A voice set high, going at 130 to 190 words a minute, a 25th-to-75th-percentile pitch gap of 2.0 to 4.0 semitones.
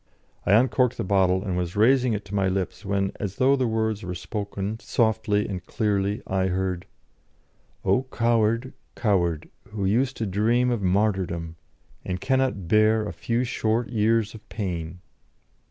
No: low, 105 Hz; average, 155 wpm; average, 3.3 semitones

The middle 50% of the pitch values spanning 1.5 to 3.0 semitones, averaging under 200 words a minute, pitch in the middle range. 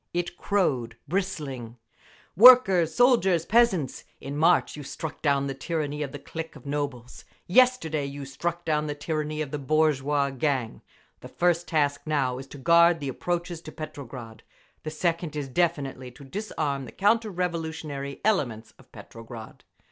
No: average, 3.9 semitones; average, 155 wpm; medium, 150 Hz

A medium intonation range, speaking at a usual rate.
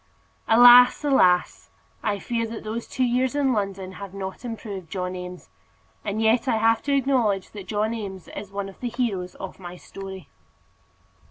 Yes: average, 3.9 semitones; average, 170 wpm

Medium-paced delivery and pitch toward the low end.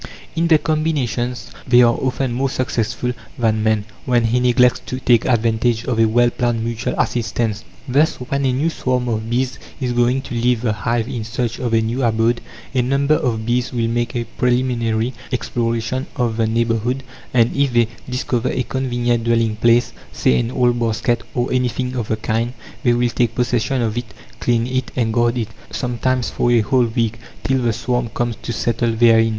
Yes: average, 190 wpm; low, 120 Hz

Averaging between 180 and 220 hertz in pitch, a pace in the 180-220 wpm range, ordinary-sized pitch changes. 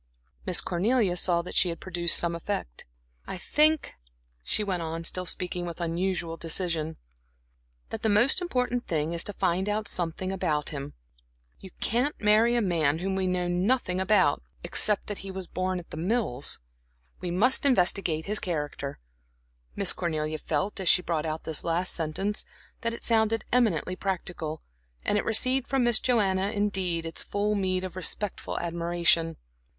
No: medium, 185 Hz; average, 165 wpm; average, 3.9 semitones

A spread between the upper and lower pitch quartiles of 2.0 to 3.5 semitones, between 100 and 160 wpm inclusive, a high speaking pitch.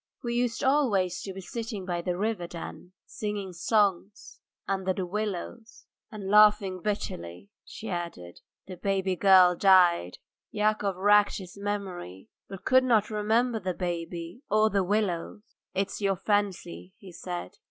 Yes: average, 2.9 semitones; average, 140 wpm; high, 195 Hz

